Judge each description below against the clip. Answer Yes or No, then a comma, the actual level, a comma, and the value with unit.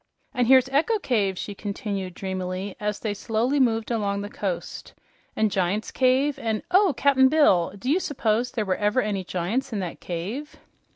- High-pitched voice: Yes, high, 215 Hz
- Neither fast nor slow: Yes, average, 175 wpm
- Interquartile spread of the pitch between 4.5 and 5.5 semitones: Yes, average, 5.0 semitones